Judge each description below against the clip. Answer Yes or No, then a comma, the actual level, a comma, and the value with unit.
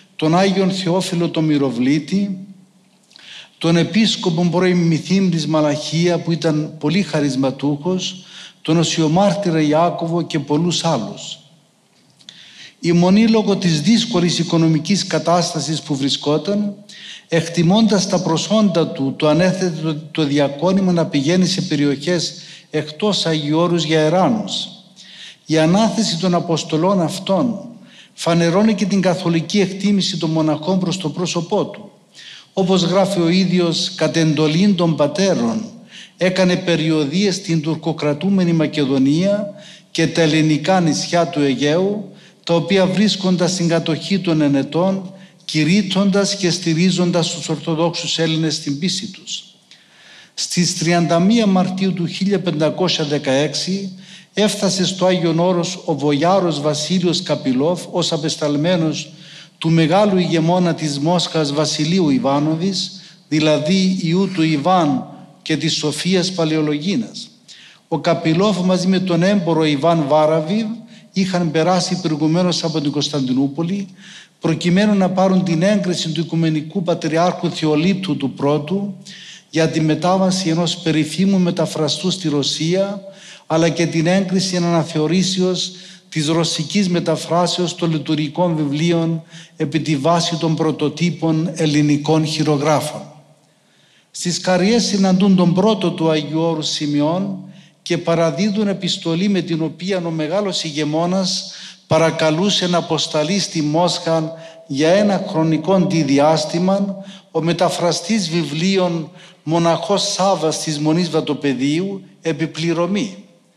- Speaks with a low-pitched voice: No, medium, 170 Hz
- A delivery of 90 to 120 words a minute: Yes, slow, 115 wpm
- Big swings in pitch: No, average, 3.1 semitones